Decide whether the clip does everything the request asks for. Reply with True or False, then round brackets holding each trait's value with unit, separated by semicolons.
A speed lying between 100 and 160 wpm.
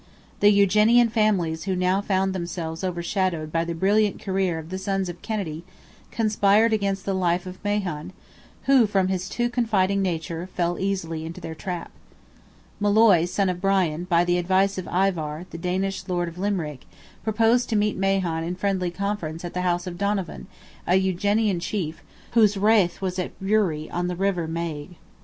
False (170 wpm)